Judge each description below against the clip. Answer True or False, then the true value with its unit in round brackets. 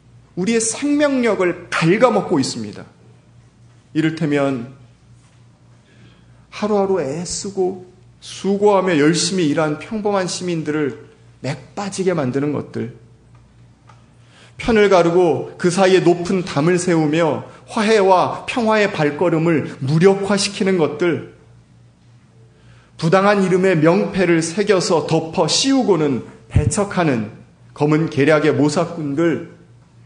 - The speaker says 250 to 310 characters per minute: False (230 characters per minute)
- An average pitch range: False (6.8 semitones)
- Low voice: False (165 Hz)